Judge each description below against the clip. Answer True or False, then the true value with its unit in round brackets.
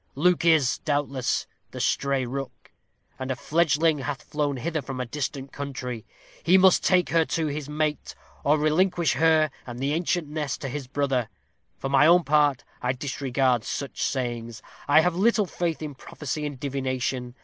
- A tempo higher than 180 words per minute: False (170 wpm)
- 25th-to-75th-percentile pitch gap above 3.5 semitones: False (3.2 semitones)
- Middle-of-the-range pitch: True (145 Hz)